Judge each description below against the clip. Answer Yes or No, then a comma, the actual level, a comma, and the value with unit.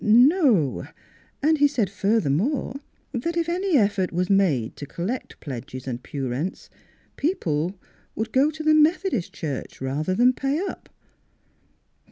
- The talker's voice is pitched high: Yes, high, 205 Hz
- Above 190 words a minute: No, average, 155 wpm